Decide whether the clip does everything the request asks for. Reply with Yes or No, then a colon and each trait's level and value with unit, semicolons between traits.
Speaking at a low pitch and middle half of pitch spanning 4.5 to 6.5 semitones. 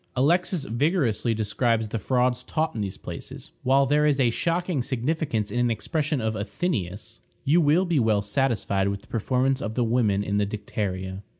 Yes: low, 120 Hz; wide, 5.4 semitones